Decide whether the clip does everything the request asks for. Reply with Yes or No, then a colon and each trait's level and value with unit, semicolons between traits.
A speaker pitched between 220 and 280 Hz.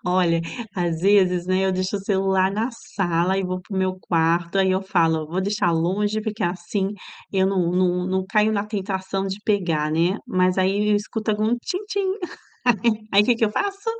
No: high, 190 Hz